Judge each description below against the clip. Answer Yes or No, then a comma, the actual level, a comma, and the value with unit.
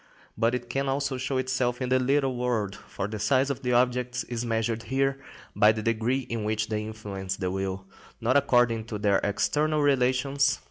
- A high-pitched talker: No, low, 120 Hz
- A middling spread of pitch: Yes, average, 3.3 semitones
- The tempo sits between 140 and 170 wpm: No, average, 190 wpm